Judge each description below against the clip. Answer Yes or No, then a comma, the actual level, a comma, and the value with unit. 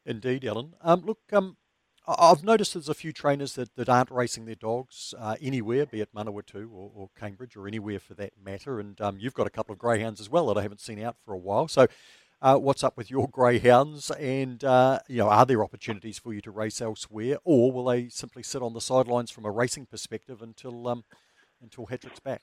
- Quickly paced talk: Yes, fast, 225 wpm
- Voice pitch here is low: Yes, low, 120 Hz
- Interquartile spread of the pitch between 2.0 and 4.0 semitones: Yes, average, 3.3 semitones